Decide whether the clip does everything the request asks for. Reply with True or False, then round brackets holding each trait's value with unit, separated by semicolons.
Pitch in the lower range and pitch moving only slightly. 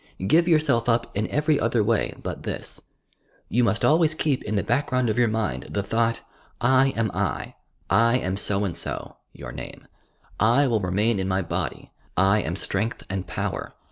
False (115 Hz; 4.0 semitones)